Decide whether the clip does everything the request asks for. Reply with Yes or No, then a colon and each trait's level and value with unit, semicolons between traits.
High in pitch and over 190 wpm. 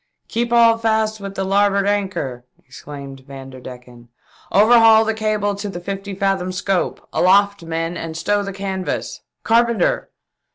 No: high, 195 Hz; average, 155 wpm